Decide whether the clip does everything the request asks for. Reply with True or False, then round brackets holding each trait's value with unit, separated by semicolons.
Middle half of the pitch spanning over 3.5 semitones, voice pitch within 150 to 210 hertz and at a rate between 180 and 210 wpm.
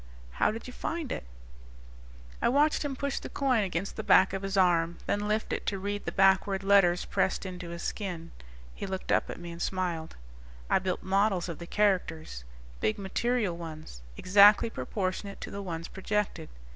False (3.0 semitones; 190 Hz; 185 wpm)